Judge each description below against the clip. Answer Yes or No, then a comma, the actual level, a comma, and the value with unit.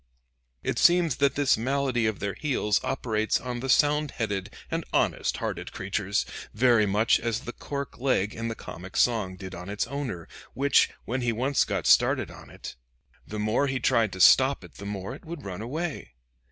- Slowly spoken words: No, average, 190 wpm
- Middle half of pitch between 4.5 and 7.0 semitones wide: Yes, average, 5.0 semitones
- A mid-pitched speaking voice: No, low, 115 Hz